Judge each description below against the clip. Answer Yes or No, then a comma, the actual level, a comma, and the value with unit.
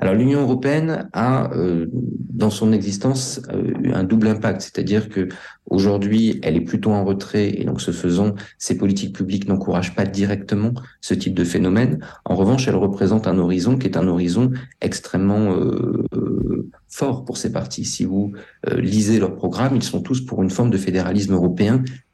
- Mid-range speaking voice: No, low, 100 Hz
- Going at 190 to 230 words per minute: No, average, 175 wpm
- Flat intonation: No, average, 3.7 semitones